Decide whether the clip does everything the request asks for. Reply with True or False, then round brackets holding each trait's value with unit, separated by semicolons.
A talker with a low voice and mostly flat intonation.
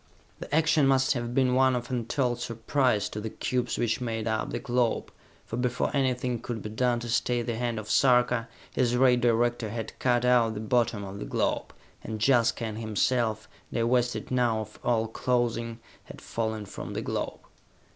True (120 Hz; 1.9 semitones)